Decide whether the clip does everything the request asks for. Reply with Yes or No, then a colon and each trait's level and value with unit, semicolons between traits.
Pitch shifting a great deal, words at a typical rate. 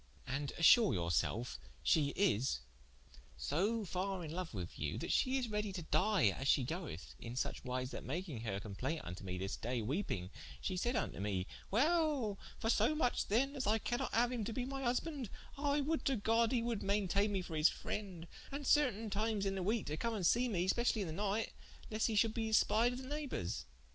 No: wide, 8.3 semitones; fast, 215 wpm